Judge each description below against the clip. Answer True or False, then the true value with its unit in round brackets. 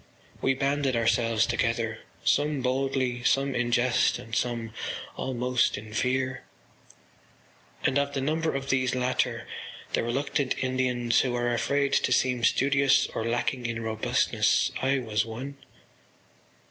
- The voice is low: True (130 Hz)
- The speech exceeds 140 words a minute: False (135 wpm)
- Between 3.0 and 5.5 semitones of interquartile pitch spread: False (2.4 semitones)